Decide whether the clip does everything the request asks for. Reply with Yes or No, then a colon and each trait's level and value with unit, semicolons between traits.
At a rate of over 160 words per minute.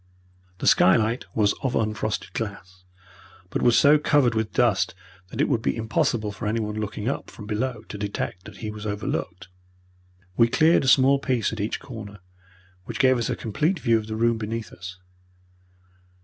Yes: average, 175 wpm